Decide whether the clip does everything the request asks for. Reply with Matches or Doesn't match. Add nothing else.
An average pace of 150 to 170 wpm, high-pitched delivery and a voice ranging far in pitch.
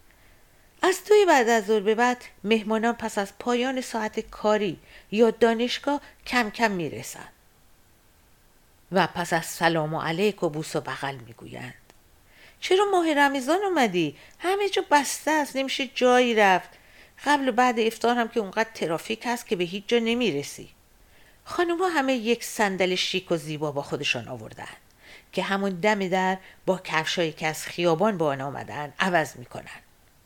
Matches